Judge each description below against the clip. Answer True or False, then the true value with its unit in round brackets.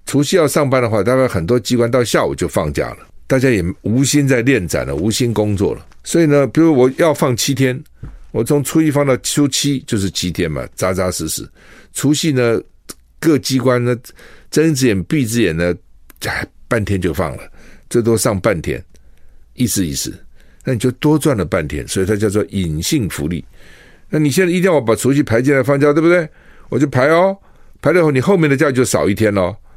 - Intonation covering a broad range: True (6.6 semitones)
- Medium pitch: False (125 Hz)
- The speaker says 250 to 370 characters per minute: True (295 characters per minute)